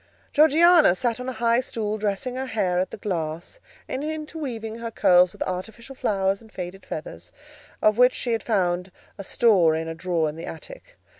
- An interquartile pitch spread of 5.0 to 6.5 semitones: Yes, wide, 5.6 semitones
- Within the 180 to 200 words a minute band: Yes, average, 190 wpm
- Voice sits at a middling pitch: No, high, 215 Hz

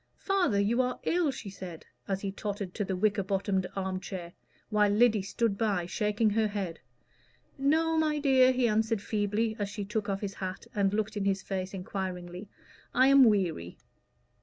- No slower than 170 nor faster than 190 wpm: Yes, average, 180 wpm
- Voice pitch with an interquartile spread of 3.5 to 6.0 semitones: No, average, 2.9 semitones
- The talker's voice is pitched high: Yes, high, 205 Hz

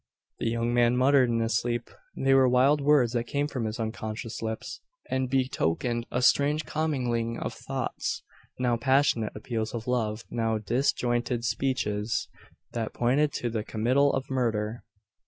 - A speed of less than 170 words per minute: Yes, average, 155 wpm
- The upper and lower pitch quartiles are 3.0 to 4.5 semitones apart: No, narrow, 2.6 semitones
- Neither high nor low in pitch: No, low, 120 Hz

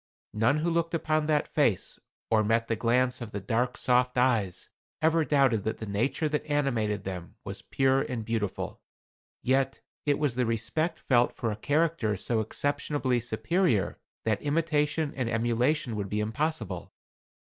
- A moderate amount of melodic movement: Yes, average, 5.0 semitones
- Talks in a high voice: No, low, 125 Hz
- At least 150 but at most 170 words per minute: Yes, average, 160 wpm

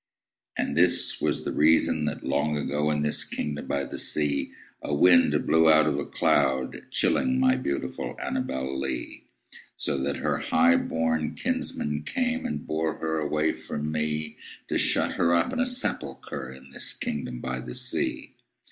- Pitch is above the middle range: No, very low, 75 Hz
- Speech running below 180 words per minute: Yes, average, 165 wpm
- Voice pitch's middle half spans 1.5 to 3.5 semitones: Yes, narrow, 2.6 semitones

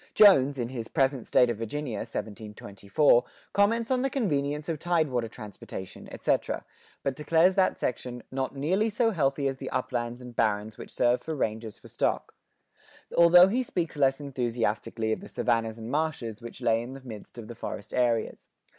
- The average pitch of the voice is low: Yes, low, 130 Hz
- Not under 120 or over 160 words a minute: No, average, 175 wpm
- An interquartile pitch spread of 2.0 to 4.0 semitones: No, average, 5.3 semitones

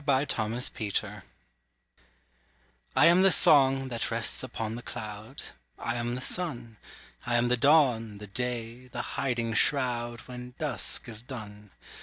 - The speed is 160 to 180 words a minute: No, average, 150 wpm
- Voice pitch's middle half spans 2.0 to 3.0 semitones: Yes, narrow, 2.6 semitones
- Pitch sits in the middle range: No, low, 120 Hz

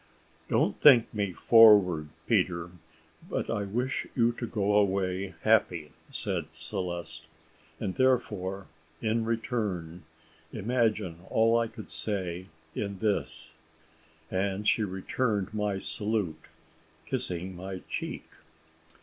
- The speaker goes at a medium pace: No, slow, 110 wpm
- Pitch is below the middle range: Yes, low, 100 Hz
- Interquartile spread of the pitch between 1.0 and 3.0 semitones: No, average, 3.6 semitones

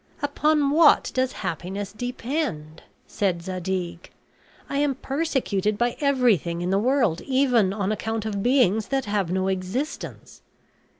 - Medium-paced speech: No, slow, 130 wpm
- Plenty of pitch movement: Yes, wide, 6.1 semitones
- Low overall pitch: No, high, 215 Hz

